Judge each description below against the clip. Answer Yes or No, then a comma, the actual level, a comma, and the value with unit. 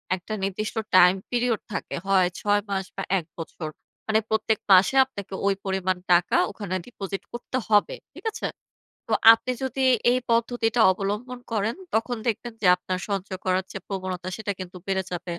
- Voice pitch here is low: No, high, 200 Hz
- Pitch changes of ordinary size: Yes, average, 3.4 semitones